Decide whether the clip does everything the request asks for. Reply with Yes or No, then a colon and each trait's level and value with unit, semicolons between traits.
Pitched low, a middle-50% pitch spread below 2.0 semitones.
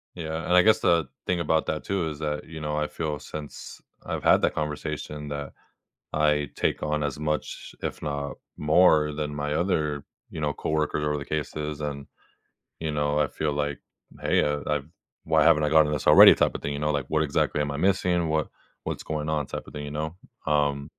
Yes: very low, 75 Hz; narrow, 1.1 semitones